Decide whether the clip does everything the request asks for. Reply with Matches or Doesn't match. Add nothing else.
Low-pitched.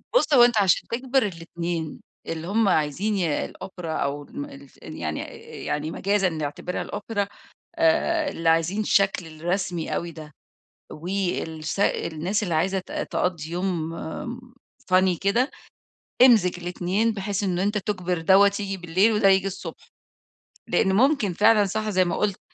Doesn't match